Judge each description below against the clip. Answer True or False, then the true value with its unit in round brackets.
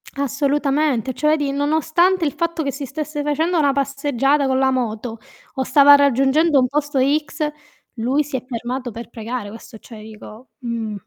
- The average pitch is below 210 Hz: False (275 Hz)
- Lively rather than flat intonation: False (3.1 semitones)